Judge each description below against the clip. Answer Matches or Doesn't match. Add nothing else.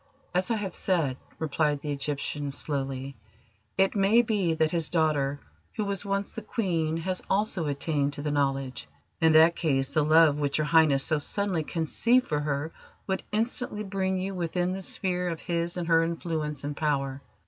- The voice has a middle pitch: Matches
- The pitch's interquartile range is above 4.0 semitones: Matches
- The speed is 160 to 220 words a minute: Matches